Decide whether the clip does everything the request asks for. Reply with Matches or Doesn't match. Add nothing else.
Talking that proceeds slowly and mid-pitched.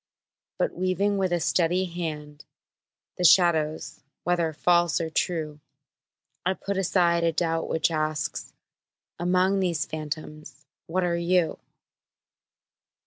Matches